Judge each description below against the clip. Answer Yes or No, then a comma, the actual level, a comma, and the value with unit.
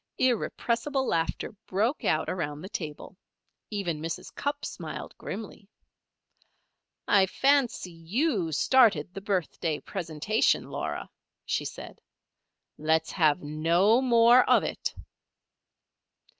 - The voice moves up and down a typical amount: No, wide, 6.4 semitones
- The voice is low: No, high, 195 Hz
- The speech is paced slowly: Yes, slow, 105 wpm